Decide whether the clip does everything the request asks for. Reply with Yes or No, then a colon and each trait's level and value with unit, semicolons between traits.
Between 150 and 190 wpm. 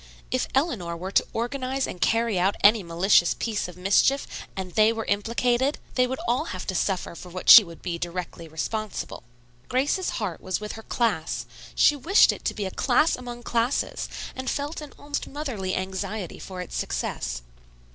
Yes: average, 180 wpm